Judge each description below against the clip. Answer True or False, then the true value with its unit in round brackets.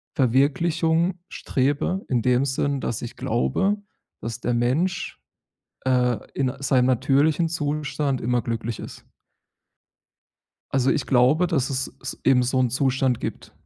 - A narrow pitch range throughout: False (3.0 semitones)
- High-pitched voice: False (135 Hz)